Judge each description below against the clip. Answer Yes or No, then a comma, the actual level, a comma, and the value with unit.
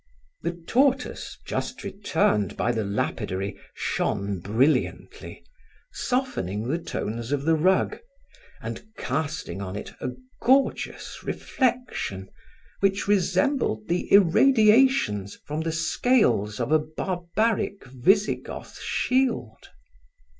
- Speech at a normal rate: No, slow, 100 wpm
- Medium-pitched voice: Yes, medium, 160 Hz